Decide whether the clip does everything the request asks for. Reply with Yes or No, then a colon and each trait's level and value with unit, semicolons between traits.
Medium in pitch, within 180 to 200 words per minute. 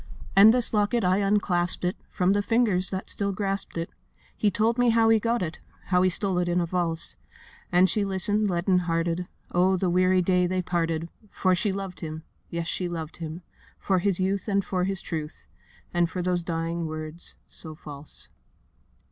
Yes: medium, 180 Hz; average, 185 wpm